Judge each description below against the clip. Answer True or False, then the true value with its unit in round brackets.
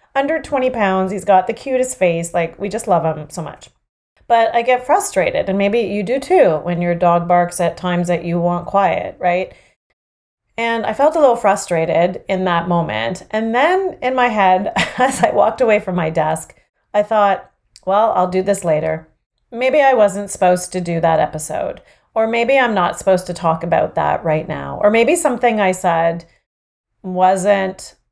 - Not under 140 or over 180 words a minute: False (190 wpm)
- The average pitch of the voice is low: False (190 Hz)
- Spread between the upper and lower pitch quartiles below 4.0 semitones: False (5.1 semitones)